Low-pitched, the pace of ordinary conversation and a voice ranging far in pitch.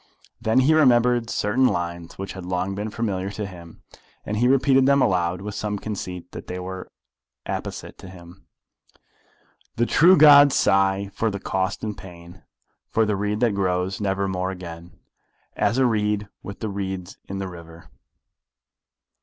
No: low, 100 Hz; average, 160 wpm; average, 3.3 semitones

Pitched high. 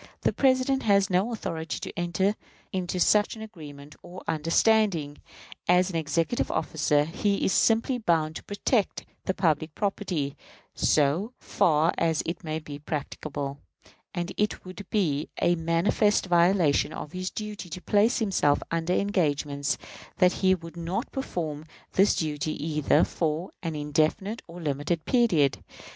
No: medium, 170 Hz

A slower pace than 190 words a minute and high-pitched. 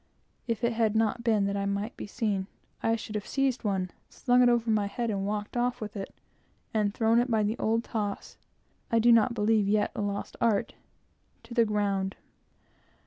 No: average, 195 wpm; high, 215 Hz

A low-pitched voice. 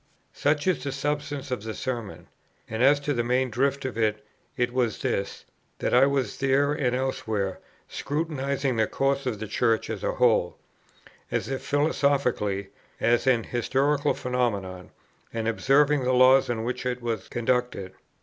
Yes: low, 125 Hz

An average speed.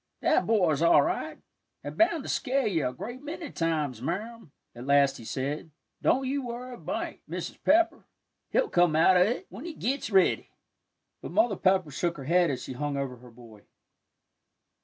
Yes: average, 185 wpm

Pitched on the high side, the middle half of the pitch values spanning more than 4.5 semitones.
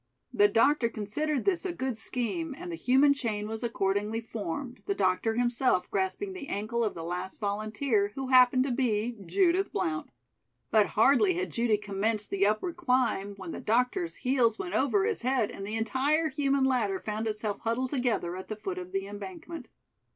Yes: high, 235 Hz; average, 5.0 semitones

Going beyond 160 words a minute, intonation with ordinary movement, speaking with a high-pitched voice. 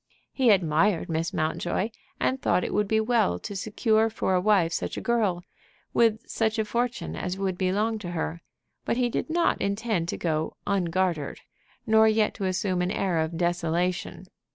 Yes: average, 175 wpm; average, 4.1 semitones; high, 195 Hz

